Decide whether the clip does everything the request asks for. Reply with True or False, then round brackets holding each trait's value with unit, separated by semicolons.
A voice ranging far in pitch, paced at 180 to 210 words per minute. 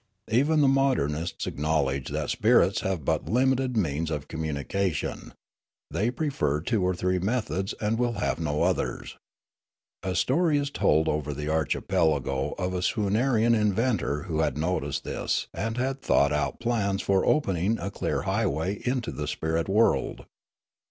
False (7.3 semitones; 150 wpm)